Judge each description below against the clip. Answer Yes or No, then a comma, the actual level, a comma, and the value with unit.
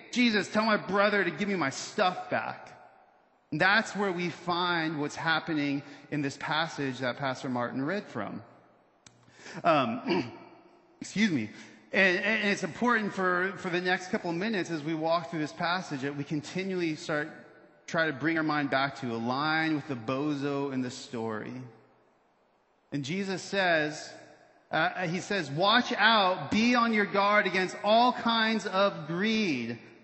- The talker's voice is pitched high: No, medium, 170 Hz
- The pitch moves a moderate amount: No, wide, 5.8 semitones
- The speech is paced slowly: No, average, 160 wpm